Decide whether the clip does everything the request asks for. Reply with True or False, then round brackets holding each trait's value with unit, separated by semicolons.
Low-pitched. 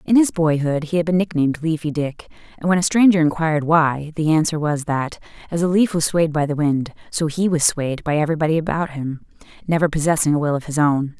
False (160 Hz)